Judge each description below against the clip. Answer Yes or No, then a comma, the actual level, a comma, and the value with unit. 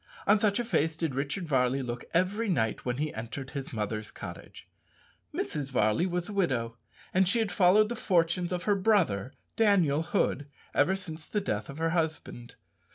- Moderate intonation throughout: No, wide, 6.6 semitones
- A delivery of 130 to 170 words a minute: No, average, 180 wpm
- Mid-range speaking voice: Yes, medium, 165 Hz